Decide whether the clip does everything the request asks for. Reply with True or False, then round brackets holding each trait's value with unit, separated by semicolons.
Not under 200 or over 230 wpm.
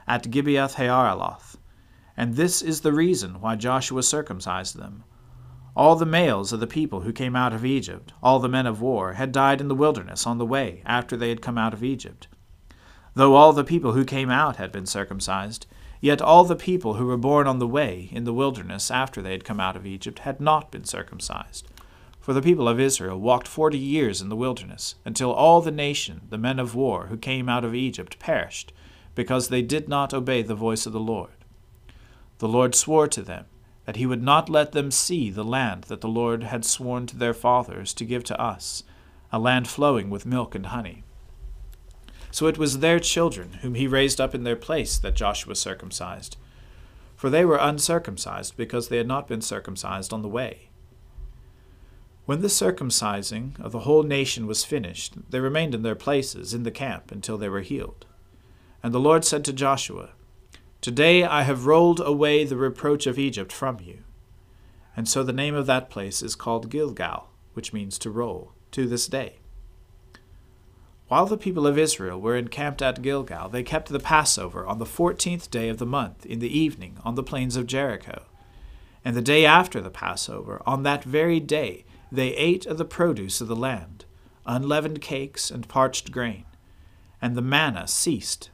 False (190 wpm)